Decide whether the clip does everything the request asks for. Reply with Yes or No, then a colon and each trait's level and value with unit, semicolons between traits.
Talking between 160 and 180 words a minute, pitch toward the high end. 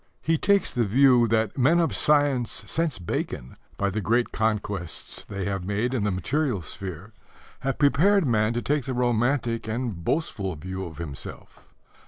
No: average, 165 wpm; low, 115 Hz